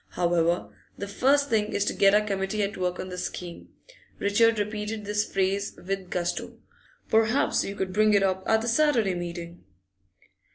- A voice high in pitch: Yes, high, 200 Hz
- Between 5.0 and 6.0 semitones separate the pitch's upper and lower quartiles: No, narrow, 2.6 semitones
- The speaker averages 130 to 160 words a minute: No, average, 170 wpm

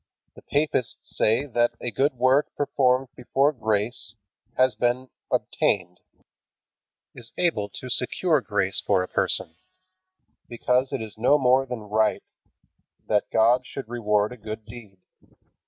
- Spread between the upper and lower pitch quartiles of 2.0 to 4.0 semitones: Yes, average, 3.3 semitones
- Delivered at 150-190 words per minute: No, slow, 135 wpm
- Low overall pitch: Yes, low, 120 Hz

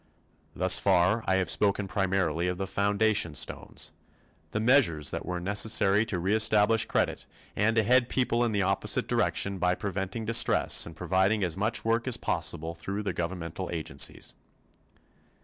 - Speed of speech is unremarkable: Yes, average, 150 wpm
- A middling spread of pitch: Yes, average, 3.5 semitones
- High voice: No, low, 100 Hz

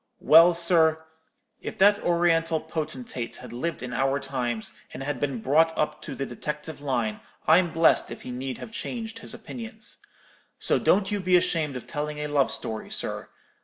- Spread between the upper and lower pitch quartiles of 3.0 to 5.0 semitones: Yes, average, 4.5 semitones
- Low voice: No, medium, 155 Hz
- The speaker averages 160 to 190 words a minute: Yes, average, 170 wpm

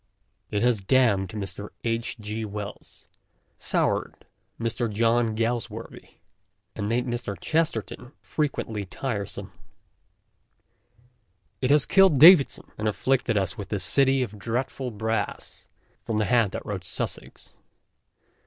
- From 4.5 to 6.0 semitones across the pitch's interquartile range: No, average, 3.4 semitones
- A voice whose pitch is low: Yes, low, 115 Hz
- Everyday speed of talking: No, slow, 125 wpm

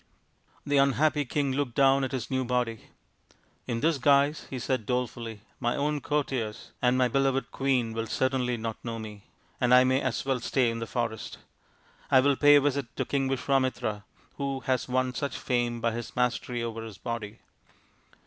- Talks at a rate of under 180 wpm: No, average, 185 wpm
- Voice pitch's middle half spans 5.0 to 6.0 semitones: No, narrow, 2.6 semitones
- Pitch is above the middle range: No, low, 125 Hz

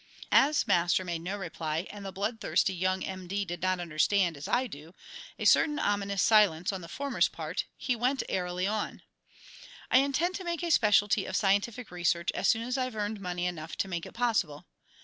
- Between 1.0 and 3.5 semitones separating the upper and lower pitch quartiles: No, average, 4.5 semitones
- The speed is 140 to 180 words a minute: No, average, 200 wpm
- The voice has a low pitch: No, high, 195 Hz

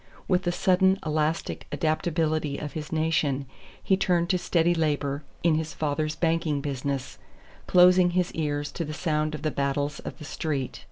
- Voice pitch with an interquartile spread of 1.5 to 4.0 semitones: Yes, average, 2.8 semitones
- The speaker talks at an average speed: Yes, average, 165 wpm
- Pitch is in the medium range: Yes, medium, 155 Hz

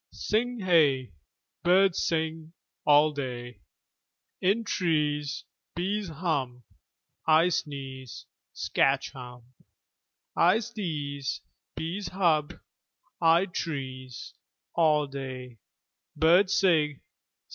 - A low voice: No, medium, 155 Hz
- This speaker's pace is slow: Yes, slow, 80 wpm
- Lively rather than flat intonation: No, average, 4.6 semitones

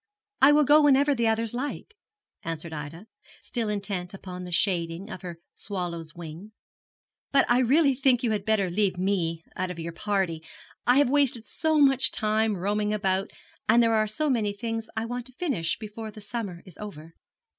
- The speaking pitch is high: Yes, high, 210 Hz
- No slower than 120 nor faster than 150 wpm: No, average, 185 wpm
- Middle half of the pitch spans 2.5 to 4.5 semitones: No, average, 5.3 semitones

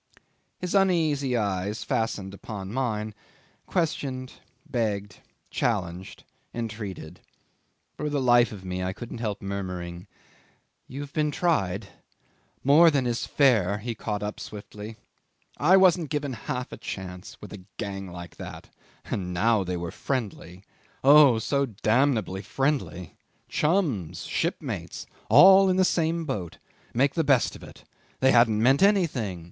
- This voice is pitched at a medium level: No, low, 115 Hz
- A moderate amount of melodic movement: No, wide, 6.4 semitones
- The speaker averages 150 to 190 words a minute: No, slow, 135 wpm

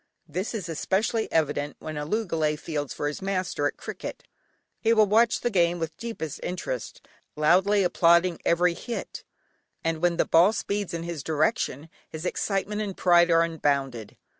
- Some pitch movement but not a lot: Yes, average, 4.0 semitones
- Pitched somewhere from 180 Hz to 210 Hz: No, medium, 170 Hz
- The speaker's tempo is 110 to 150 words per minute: No, average, 165 wpm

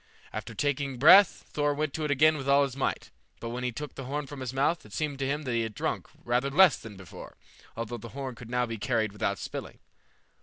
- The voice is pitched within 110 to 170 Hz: Yes, low, 135 Hz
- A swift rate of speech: Yes, fast, 240 wpm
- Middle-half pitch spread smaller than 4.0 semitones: Yes, average, 3.5 semitones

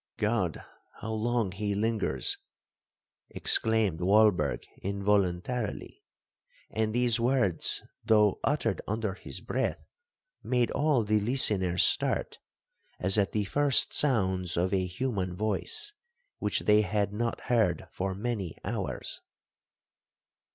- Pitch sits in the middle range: No, low, 105 Hz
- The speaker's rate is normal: No, slow, 110 wpm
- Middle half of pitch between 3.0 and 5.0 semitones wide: Yes, average, 3.6 semitones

